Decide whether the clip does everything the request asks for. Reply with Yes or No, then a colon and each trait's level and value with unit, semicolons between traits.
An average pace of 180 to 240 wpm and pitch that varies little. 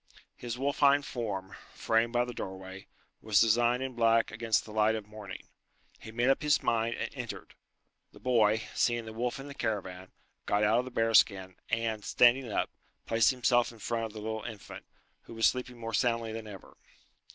Yes: average, 190 wpm; narrow, 2.0 semitones